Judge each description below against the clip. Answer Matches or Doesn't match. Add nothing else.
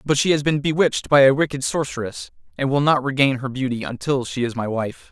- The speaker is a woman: Doesn't match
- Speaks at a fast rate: Matches